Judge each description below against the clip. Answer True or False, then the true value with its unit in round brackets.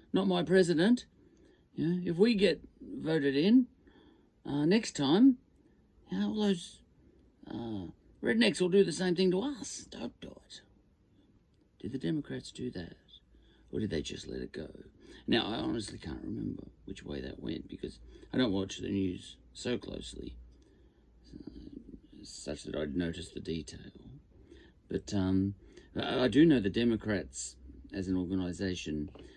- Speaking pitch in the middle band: False (105 Hz)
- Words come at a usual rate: True (150 wpm)